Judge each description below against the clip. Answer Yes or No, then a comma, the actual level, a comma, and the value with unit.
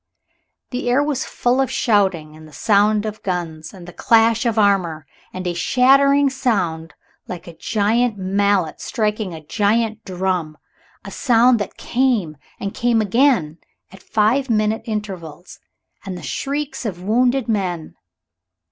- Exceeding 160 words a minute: No, average, 145 wpm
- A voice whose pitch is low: No, high, 210 Hz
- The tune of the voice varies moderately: Yes, average, 5.0 semitones